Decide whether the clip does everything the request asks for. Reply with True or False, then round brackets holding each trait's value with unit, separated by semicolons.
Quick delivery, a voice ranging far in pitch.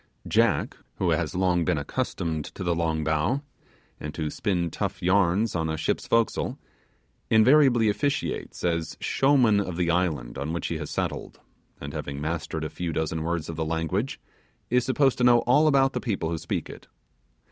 False (180 wpm; 6.3 semitones)